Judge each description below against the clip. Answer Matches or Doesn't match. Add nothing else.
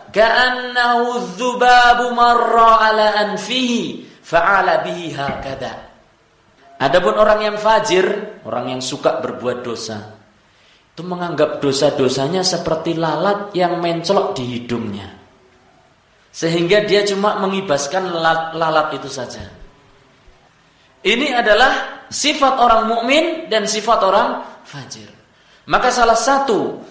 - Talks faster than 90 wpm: Doesn't match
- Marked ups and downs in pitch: Matches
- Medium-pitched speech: Doesn't match